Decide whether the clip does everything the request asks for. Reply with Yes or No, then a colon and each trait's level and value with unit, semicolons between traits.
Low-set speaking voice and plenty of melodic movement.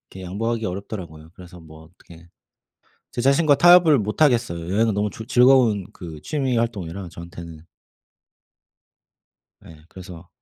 Yes: low, 100 Hz; wide, 5.8 semitones